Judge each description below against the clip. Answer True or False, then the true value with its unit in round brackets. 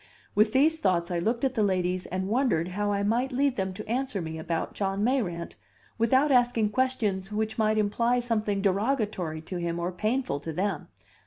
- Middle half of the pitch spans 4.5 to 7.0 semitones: True (4.9 semitones)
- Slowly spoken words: False (185 wpm)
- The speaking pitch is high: True (210 Hz)